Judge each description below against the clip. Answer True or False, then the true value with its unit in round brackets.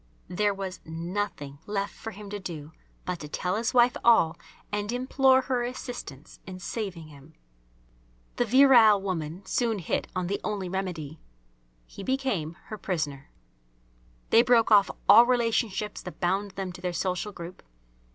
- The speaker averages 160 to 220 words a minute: False (150 wpm)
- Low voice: False (195 Hz)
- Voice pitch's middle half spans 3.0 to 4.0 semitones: False (4.5 semitones)